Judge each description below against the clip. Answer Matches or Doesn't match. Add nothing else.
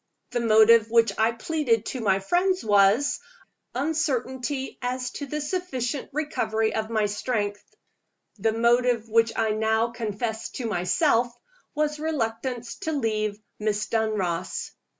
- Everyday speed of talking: Doesn't match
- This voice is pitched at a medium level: Doesn't match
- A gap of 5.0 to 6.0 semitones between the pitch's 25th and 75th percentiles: Doesn't match